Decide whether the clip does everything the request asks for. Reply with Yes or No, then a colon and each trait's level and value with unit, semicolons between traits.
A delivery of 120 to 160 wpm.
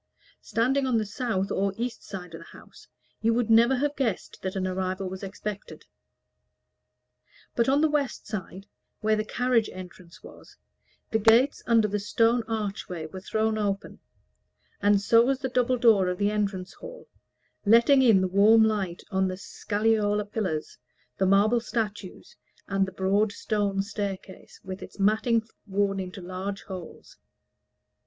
Yes: average, 155 wpm